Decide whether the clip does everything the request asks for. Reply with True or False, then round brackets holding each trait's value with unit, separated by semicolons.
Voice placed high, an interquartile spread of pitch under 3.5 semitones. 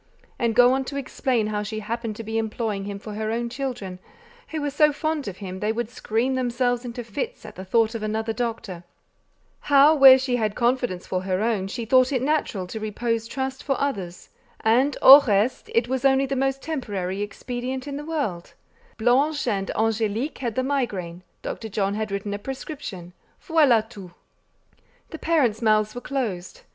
False (235 Hz; 4.1 semitones)